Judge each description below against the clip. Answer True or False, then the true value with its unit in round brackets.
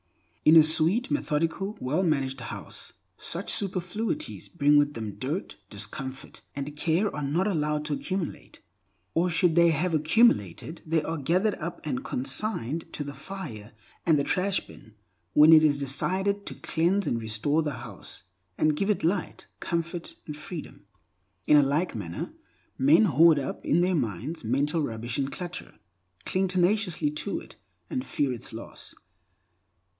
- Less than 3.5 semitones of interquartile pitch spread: False (4.5 semitones)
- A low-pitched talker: False (155 Hz)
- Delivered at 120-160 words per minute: True (155 wpm)